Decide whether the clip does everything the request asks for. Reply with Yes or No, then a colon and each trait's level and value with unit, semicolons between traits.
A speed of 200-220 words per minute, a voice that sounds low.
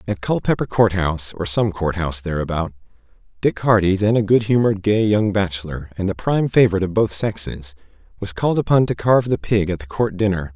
Yes: fast, 205 wpm; very low, 95 Hz